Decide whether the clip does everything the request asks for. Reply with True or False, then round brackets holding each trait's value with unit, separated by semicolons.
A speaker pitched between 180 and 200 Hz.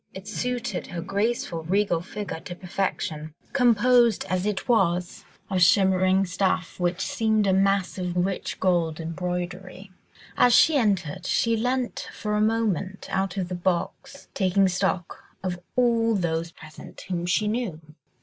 True (190 Hz)